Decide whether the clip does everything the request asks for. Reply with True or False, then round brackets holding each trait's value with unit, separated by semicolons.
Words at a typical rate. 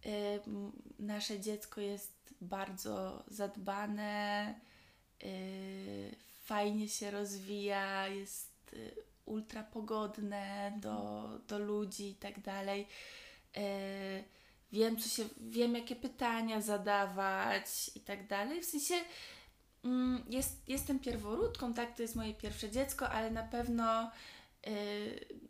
False (95 wpm)